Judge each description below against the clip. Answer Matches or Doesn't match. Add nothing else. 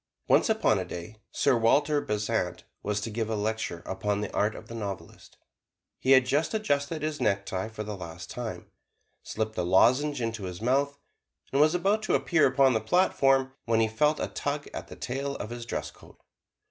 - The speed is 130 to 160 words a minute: Doesn't match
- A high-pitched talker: Doesn't match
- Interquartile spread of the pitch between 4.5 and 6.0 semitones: Matches